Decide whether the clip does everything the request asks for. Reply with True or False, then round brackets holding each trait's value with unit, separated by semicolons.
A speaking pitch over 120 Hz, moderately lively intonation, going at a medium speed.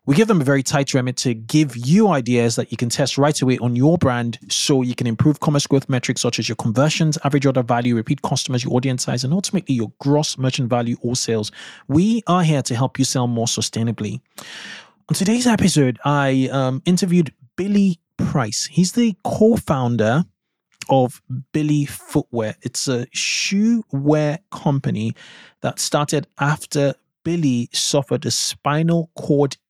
True (140 Hz; 4.3 semitones; 170 wpm)